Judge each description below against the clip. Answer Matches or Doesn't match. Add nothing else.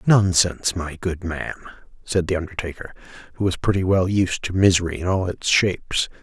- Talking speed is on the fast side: Doesn't match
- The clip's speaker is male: Matches